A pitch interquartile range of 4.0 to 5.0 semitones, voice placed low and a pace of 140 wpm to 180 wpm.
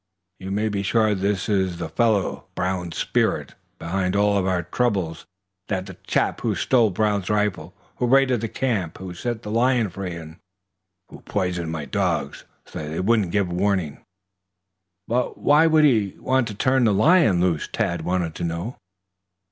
Yes: average, 4.4 semitones; low, 100 Hz; average, 165 wpm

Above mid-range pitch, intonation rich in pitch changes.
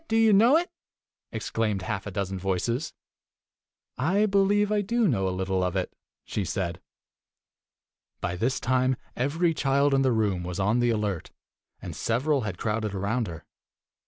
No: low, 115 Hz; wide, 8.3 semitones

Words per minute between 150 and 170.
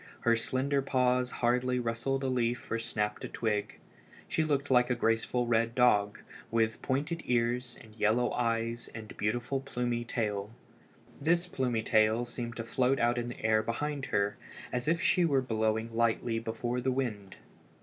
Yes: average, 165 wpm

